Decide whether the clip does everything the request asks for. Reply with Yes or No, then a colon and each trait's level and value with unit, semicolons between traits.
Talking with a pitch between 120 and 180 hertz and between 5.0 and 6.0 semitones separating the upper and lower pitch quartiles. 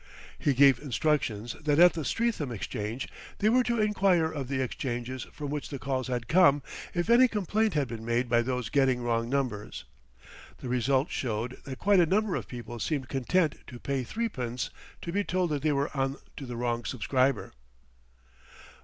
Yes: low, 135 Hz; wide, 5.4 semitones